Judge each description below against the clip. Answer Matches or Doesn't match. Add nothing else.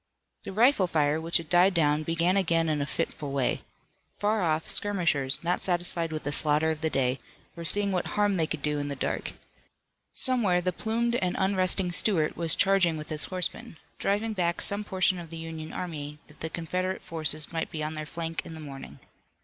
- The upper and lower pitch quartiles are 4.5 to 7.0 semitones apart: Doesn't match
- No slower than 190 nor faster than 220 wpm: Matches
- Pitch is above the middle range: Doesn't match